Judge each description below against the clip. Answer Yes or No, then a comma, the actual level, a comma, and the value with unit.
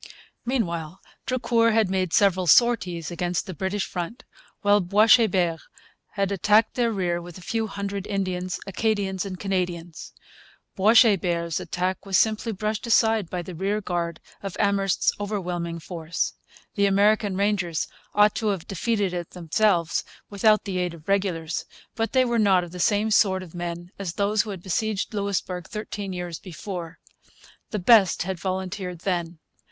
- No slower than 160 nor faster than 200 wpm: No, average, 150 wpm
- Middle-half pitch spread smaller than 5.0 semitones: Yes, average, 3.0 semitones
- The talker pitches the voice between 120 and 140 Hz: No, high, 190 Hz